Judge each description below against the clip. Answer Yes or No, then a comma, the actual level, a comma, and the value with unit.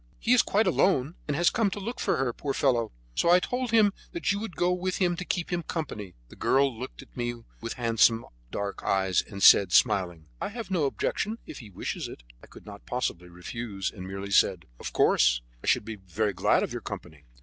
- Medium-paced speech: No, fast, 225 wpm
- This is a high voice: No, low, 120 Hz